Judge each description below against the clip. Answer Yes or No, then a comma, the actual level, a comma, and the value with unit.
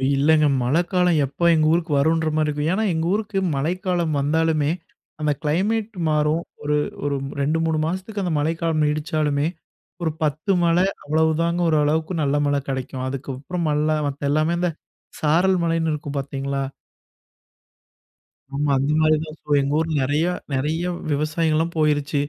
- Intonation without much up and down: Yes, narrow, 2.3 semitones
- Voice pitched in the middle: Yes, medium, 155 Hz